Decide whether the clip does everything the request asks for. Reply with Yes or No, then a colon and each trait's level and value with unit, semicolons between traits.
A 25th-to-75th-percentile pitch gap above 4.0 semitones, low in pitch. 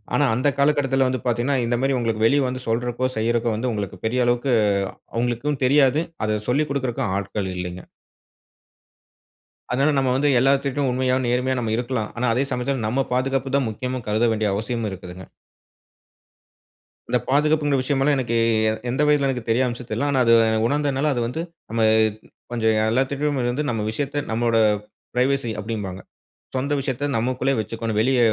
No: average, 3.1 semitones; low, 125 Hz